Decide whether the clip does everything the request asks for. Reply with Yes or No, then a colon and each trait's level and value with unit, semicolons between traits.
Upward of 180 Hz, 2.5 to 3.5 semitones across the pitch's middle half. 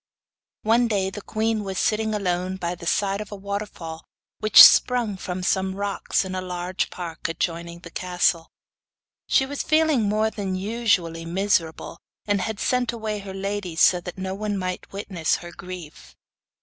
Yes: high, 190 Hz; average, 3.0 semitones